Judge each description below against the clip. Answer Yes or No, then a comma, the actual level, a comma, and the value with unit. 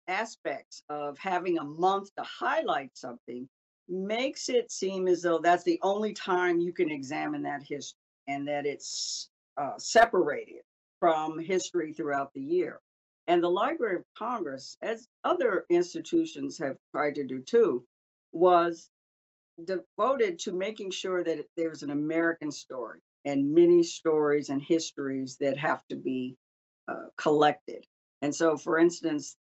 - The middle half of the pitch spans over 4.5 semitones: Yes, wide, 5.4 semitones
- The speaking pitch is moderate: Yes, medium, 170 Hz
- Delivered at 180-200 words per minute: No, average, 145 wpm